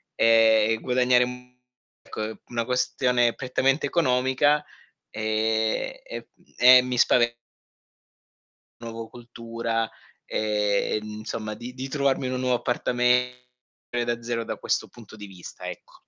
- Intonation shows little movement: Yes, narrow, 2.0 semitones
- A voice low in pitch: Yes, low, 120 Hz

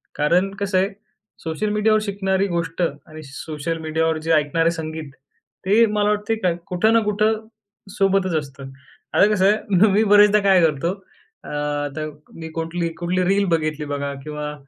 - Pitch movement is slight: No, average, 4.5 semitones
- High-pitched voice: No, medium, 175 Hz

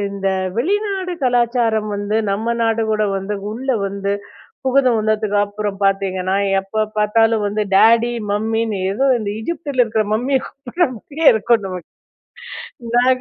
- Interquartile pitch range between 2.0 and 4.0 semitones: Yes, average, 3.3 semitones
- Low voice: No, high, 220 Hz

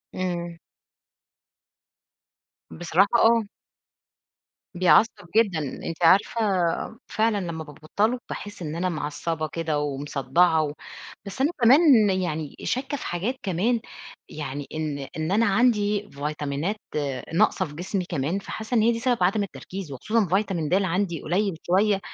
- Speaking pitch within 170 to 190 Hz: Yes, medium, 185 Hz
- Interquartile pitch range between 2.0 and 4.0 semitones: No, average, 5.0 semitones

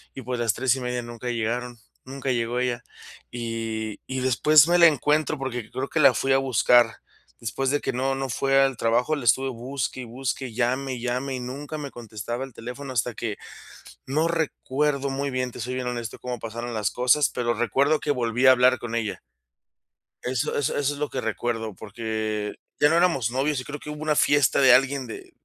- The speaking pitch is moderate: No, low, 125 Hz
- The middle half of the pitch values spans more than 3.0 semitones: No, narrow, 2.6 semitones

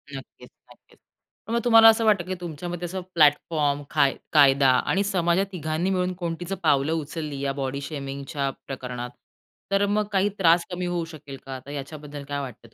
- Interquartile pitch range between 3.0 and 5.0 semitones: Yes, average, 4.5 semitones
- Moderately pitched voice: Yes, medium, 155 Hz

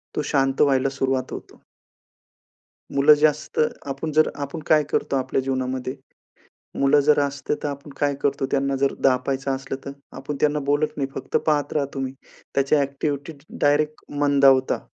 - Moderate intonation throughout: No, narrow, 1.5 semitones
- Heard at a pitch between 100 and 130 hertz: No, medium, 140 Hz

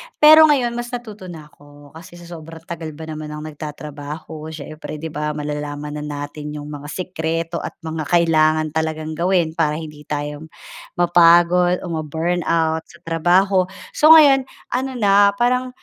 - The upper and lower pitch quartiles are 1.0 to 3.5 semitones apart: Yes, average, 3.0 semitones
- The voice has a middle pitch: Yes, medium, 160 Hz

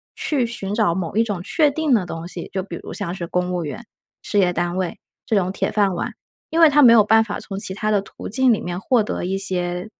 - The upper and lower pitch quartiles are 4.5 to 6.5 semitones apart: No, average, 4.0 semitones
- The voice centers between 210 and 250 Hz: No, high, 195 Hz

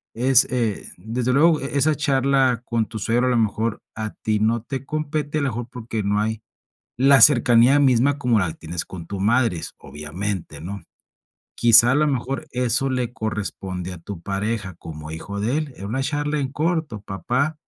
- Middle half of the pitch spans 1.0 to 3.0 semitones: No, average, 4.9 semitones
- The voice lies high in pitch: No, low, 120 Hz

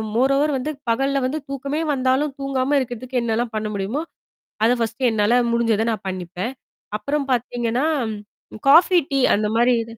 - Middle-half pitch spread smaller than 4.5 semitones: Yes, average, 3.3 semitones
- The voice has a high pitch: Yes, very high, 250 Hz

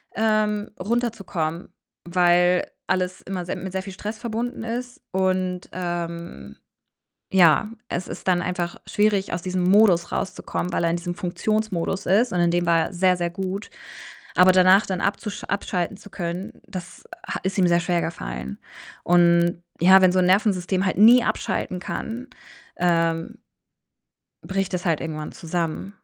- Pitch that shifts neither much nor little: No, narrow, 2.2 semitones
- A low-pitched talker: No, medium, 185 Hz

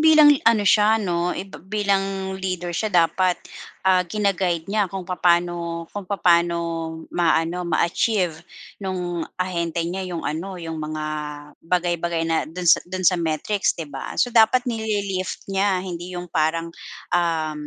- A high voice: No, medium, 180 Hz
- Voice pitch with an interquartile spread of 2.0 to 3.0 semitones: Yes, narrow, 2.5 semitones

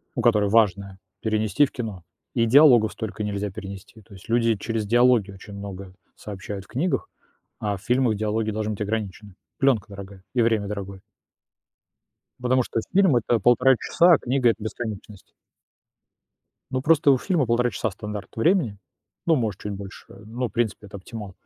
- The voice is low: Yes, low, 110 Hz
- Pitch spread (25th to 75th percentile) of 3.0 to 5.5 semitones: Yes, average, 3.3 semitones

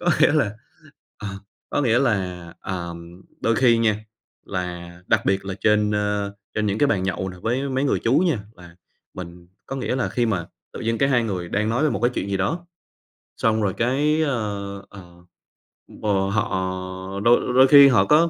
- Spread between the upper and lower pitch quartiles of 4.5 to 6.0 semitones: Yes, average, 4.9 semitones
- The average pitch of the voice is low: Yes, low, 105 Hz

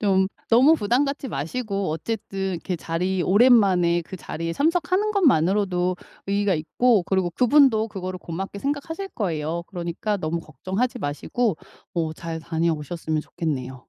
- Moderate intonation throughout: No, wide, 5.7 semitones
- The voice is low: No, high, 190 Hz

